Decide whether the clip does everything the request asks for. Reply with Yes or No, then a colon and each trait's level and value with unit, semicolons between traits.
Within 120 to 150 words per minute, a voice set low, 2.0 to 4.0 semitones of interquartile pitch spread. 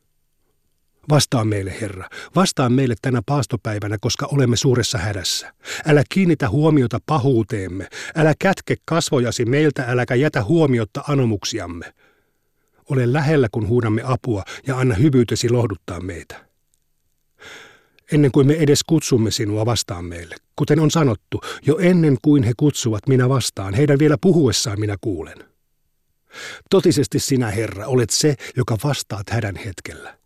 No: average, 130 wpm; low, 125 Hz; average, 5.0 semitones